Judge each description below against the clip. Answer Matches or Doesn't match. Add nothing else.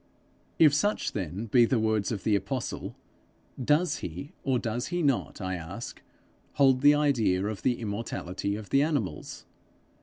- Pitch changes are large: Matches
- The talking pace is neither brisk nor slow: Matches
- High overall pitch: Doesn't match